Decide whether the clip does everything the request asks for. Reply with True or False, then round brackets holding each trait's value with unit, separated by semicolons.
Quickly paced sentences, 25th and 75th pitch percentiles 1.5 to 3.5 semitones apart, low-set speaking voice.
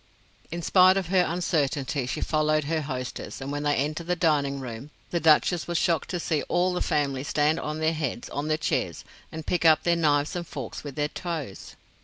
False (210 wpm; 2.9 semitones; 155 Hz)